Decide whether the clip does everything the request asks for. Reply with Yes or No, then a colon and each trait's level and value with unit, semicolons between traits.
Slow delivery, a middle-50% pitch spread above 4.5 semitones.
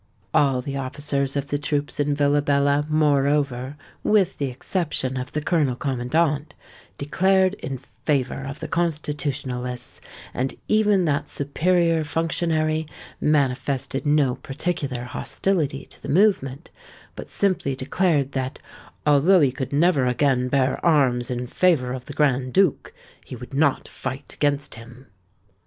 No: slow, 130 wpm; average, 2.9 semitones